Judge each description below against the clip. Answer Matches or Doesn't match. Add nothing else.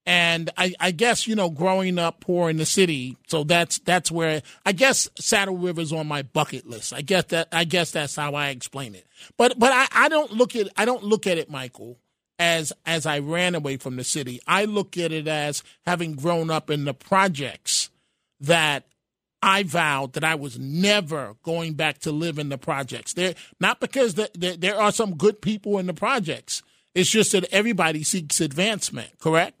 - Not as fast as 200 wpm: Doesn't match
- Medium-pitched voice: Matches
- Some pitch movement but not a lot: Matches